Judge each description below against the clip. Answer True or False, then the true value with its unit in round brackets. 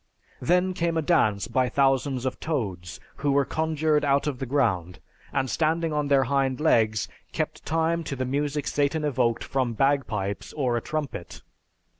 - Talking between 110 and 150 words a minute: False (165 wpm)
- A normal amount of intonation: True (3.7 semitones)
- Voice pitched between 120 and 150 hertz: True (140 Hz)